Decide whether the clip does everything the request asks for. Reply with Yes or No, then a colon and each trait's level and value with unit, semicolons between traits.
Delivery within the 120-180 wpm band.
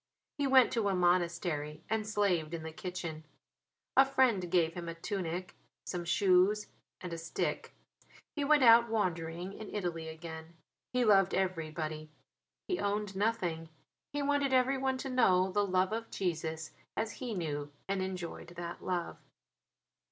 Yes: average, 150 wpm